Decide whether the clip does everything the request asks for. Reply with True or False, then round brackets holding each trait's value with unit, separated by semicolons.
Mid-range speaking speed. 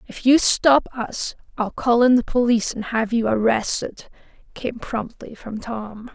True (165 wpm)